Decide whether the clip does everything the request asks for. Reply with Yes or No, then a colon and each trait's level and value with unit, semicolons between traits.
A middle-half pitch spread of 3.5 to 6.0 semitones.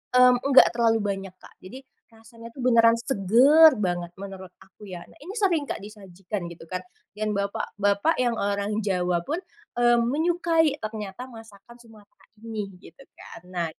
Yes: average, 4.3 semitones